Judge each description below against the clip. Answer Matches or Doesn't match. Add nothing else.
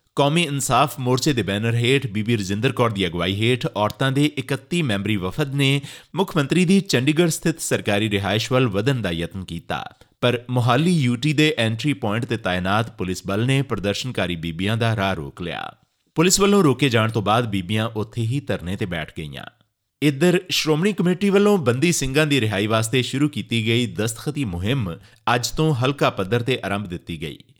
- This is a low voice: Matches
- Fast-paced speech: Matches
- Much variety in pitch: Matches